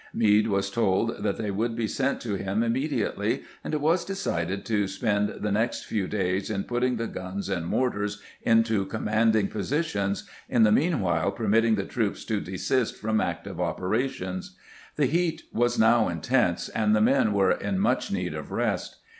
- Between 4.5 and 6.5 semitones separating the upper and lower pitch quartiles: No, average, 3.4 semitones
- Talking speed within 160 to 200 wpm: Yes, average, 180 wpm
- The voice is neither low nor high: No, low, 110 Hz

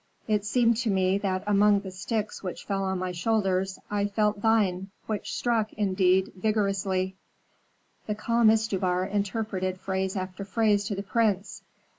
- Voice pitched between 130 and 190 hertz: No, high, 200 Hz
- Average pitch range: No, narrow, 2.2 semitones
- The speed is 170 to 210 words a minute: No, average, 150 wpm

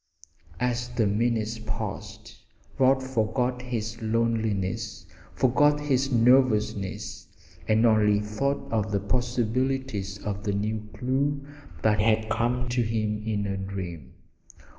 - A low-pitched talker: Yes, low, 110 Hz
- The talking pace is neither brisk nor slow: No, slow, 120 wpm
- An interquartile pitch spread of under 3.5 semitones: Yes, average, 2.9 semitones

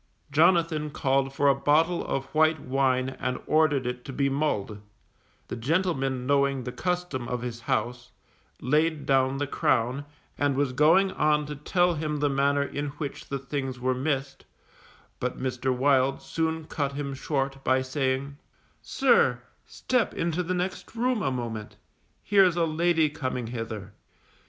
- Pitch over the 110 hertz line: Yes, medium, 140 Hz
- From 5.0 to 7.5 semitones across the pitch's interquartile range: No, average, 3.3 semitones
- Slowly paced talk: No, average, 155 wpm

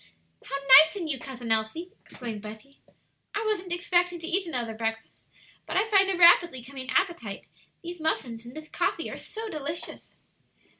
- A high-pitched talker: Yes, very high, 310 Hz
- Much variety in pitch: Yes, wide, 6.7 semitones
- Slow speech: No, average, 165 wpm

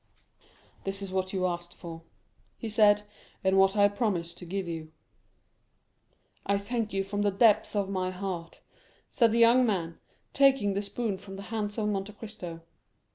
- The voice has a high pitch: Yes, high, 200 Hz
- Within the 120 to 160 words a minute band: No, average, 170 wpm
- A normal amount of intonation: No, narrow, 2.2 semitones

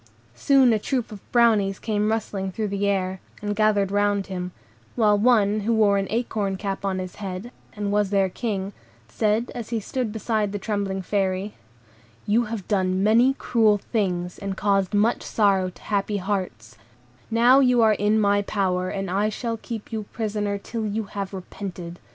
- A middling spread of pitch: No, narrow, 2.1 semitones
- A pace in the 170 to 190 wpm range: Yes, average, 175 wpm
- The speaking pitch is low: No, high, 205 Hz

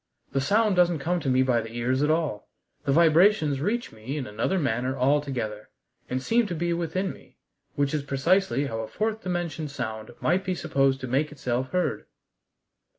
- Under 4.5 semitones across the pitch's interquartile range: No, average, 5.3 semitones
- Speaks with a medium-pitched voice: Yes, medium, 145 Hz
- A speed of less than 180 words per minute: No, average, 185 wpm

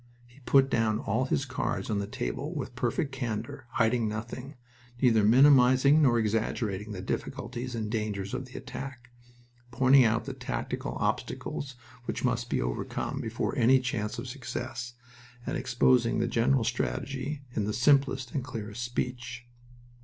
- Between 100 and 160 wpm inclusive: Yes, average, 150 wpm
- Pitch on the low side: Yes, low, 120 Hz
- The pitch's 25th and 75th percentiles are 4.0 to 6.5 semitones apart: No, average, 2.9 semitones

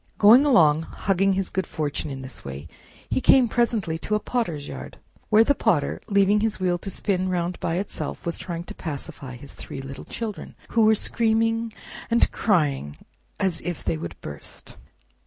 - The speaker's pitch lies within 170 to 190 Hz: Yes, medium, 185 Hz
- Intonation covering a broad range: Yes, wide, 6.8 semitones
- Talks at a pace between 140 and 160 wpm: No, average, 175 wpm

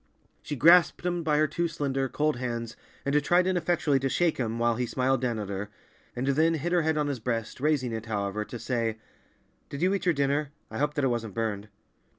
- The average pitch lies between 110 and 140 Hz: Yes, low, 135 Hz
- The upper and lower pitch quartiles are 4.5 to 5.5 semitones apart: Yes, average, 4.8 semitones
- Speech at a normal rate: No, fast, 220 wpm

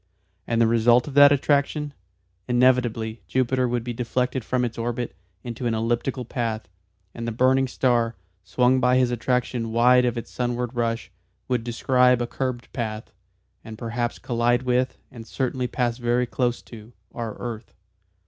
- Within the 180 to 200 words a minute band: No, average, 160 wpm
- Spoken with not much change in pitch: Yes, narrow, 1.4 semitones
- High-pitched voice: No, low, 120 Hz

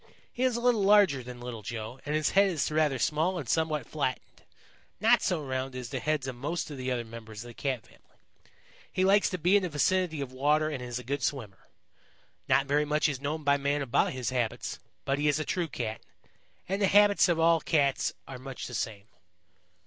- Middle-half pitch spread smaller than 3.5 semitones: No, average, 4.4 semitones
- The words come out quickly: Yes, fast, 220 wpm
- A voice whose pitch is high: No, medium, 145 Hz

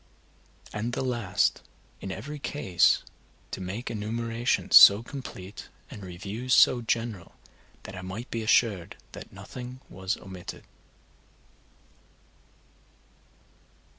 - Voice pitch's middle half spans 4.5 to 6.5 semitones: No, average, 4.1 semitones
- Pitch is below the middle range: Yes, low, 110 Hz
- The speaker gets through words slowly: Yes, slow, 105 wpm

